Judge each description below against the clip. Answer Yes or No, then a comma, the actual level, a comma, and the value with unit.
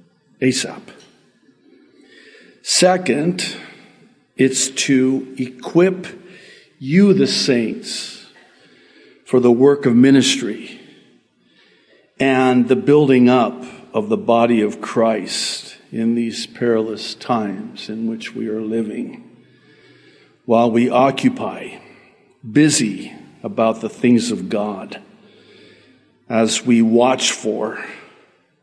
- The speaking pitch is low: Yes, low, 125 Hz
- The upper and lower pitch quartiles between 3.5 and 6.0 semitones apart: No, average, 2.8 semitones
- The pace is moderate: No, slow, 90 wpm